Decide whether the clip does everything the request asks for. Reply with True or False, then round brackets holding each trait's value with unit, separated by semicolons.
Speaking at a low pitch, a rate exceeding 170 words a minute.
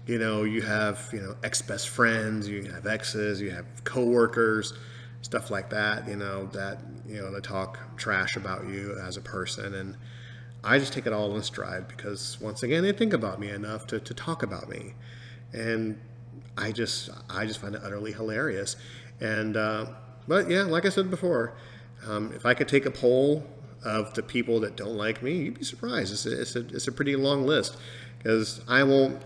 True (115 Hz; 200 wpm)